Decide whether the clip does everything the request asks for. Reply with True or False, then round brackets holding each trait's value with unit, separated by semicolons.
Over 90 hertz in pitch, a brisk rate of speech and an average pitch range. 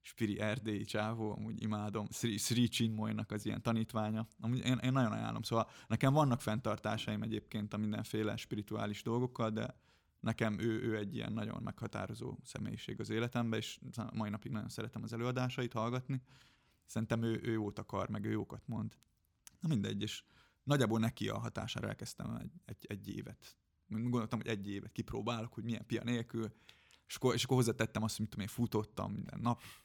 False (110 Hz; 170 wpm; 1.7 semitones)